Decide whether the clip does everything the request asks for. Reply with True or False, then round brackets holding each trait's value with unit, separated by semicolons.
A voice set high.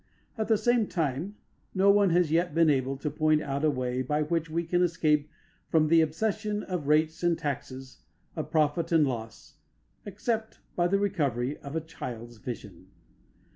False (155 Hz)